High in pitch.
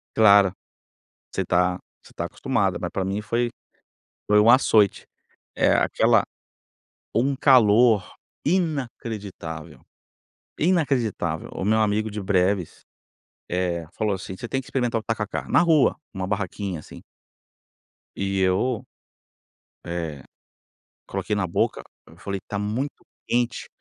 No: low, 105 Hz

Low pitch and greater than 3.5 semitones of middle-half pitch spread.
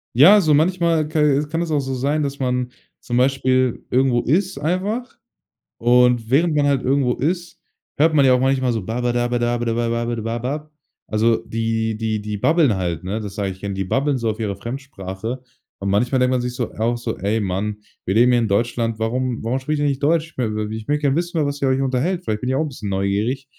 Yes: low, 125 Hz; average, 4.1 semitones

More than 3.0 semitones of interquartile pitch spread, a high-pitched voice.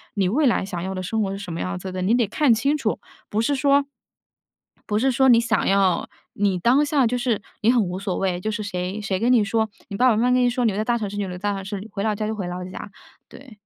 Yes: average, 3.8 semitones; high, 215 Hz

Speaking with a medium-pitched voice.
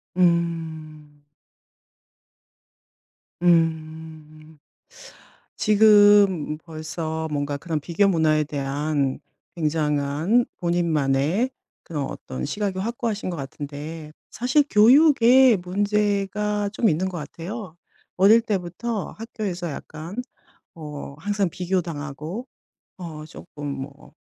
Yes: medium, 170 Hz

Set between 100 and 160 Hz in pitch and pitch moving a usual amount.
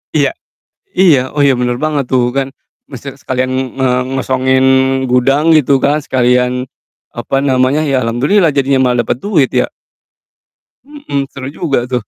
No: low, 135 Hz; narrow, 2.2 semitones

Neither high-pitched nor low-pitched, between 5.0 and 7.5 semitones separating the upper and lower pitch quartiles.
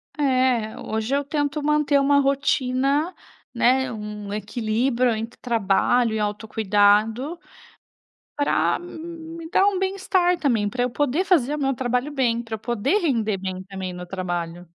No: very high, 250 Hz; average, 5.3 semitones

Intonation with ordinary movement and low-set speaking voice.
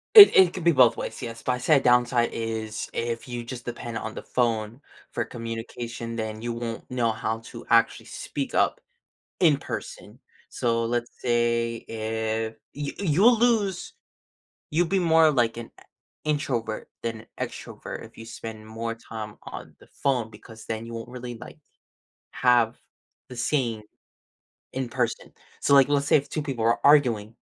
Yes: average, 3.3 semitones; low, 120 Hz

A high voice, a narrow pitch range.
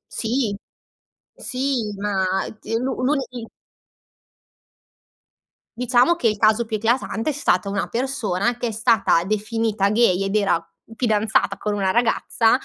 No: high, 225 Hz; average, 3.1 semitones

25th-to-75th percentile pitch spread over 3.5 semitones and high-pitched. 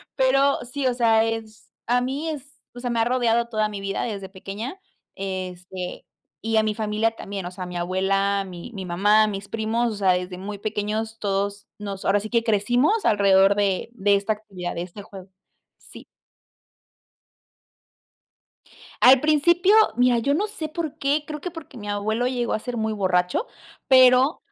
Yes: average, 4.1 semitones; high, 215 Hz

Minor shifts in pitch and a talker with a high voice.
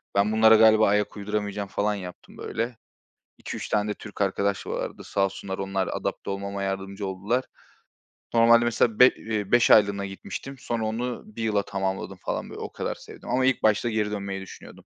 No: narrow, 2.2 semitones; low, 105 Hz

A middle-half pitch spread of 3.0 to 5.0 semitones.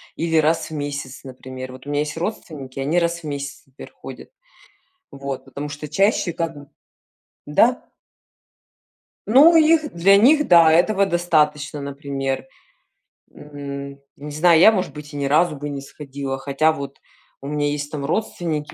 Yes: average, 3.3 semitones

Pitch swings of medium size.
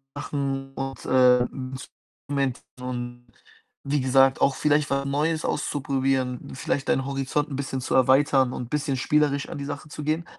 No: narrow, 1.7 semitones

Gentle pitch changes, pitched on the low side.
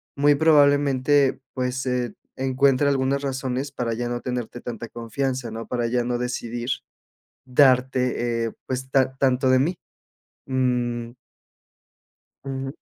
Yes: narrow, 1.9 semitones; low, 130 Hz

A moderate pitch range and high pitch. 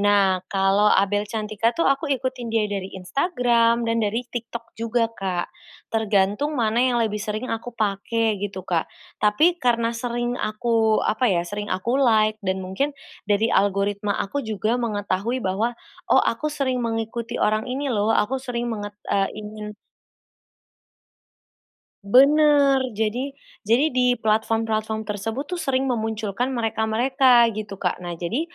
Yes: average, 3.2 semitones; high, 225 Hz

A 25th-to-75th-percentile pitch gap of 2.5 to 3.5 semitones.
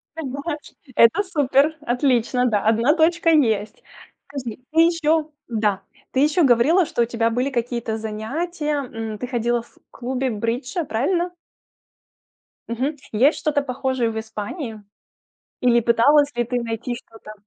No: average, 4.6 semitones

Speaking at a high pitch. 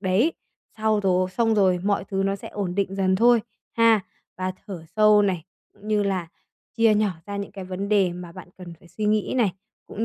Yes: high, 200 Hz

